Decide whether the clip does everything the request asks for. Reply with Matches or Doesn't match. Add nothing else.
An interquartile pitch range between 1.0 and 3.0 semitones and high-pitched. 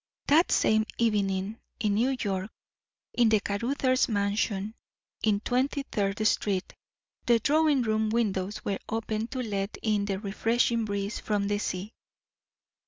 Matches